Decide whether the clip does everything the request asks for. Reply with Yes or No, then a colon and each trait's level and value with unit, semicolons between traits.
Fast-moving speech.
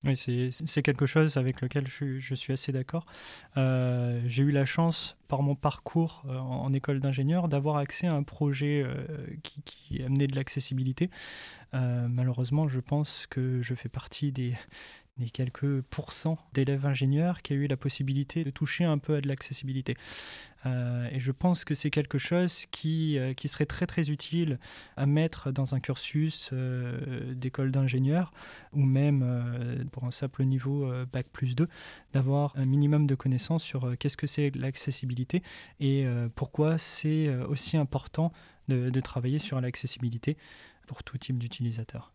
No: average, 170 wpm